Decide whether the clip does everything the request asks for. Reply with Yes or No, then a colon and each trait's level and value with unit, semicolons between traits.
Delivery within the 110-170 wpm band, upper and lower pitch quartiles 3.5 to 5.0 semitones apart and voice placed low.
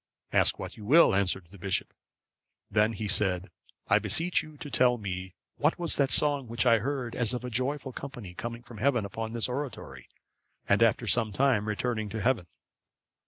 No: average, 185 wpm; average, 4.2 semitones; low, 115 Hz